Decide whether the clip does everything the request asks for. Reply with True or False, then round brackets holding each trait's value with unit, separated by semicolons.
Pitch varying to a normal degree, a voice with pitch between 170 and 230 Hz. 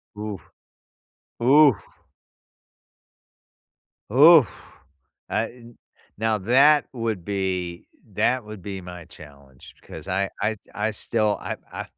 False (4.2 semitones; 105 Hz)